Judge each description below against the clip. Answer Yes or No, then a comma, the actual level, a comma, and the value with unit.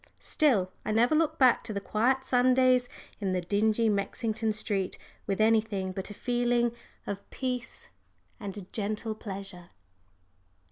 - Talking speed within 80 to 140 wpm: Yes, slow, 135 wpm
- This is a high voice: Yes, high, 220 Hz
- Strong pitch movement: No, average, 3.6 semitones